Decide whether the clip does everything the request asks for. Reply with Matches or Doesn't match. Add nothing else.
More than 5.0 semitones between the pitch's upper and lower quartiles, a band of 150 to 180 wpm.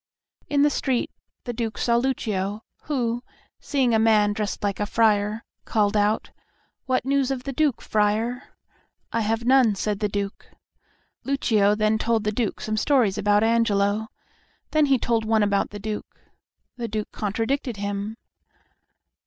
Doesn't match